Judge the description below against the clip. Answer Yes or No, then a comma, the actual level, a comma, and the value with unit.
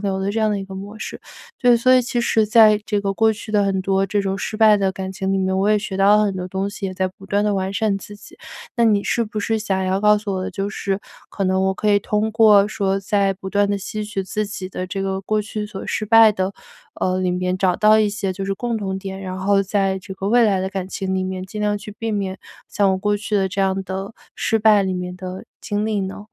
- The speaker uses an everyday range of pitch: No, narrow, 1.8 semitones